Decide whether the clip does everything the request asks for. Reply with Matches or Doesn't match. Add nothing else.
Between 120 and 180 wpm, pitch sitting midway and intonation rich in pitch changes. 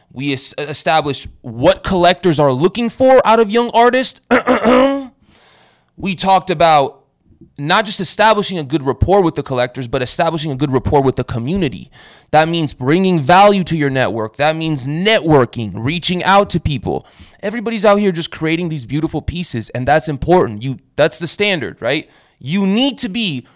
Matches